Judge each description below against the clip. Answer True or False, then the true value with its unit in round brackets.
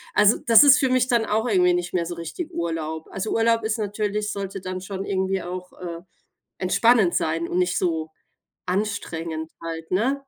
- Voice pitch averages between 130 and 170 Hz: False (190 Hz)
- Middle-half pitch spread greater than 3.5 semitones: True (4.2 semitones)